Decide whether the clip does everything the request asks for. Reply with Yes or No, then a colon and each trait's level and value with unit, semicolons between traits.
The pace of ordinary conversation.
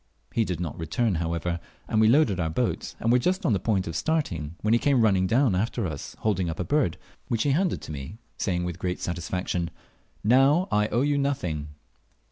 No: fast, 210 wpm